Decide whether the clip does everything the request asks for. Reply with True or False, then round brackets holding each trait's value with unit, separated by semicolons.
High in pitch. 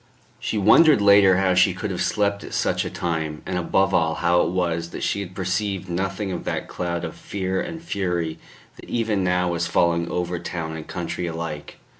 False (90 Hz)